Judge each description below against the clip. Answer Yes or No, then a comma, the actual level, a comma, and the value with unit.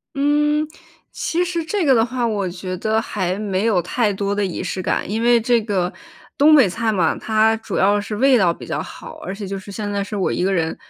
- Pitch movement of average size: Yes, average, 4.0 semitones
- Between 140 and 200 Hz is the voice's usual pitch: No, high, 210 Hz